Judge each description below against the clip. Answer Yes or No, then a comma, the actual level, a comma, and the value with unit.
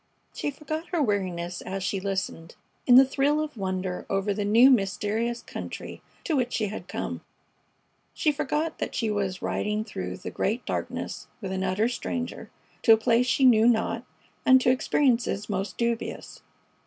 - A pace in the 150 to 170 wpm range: Yes, average, 165 wpm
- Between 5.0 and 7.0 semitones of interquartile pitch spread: No, average, 4.6 semitones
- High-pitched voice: Yes, high, 220 Hz